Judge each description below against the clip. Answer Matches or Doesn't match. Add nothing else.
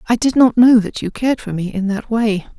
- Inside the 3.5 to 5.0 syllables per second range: Doesn't match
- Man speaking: Doesn't match